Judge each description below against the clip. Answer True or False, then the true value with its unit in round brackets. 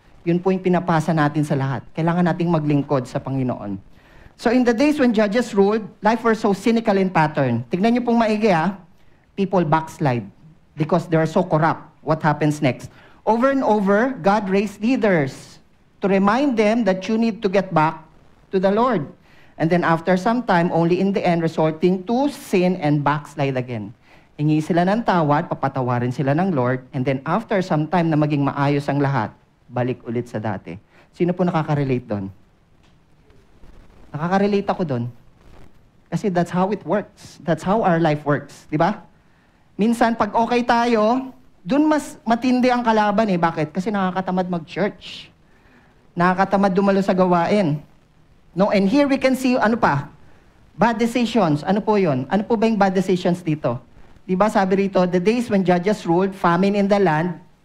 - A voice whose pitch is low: False (180 Hz)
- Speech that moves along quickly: True (170 wpm)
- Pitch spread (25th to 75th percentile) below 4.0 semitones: False (5.6 semitones)